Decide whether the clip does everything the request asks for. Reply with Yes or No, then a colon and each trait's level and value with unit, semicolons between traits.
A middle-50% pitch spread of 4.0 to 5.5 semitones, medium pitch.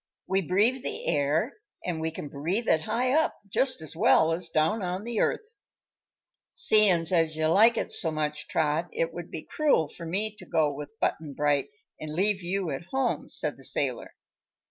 Yes: average, 5.2 semitones; medium, 170 Hz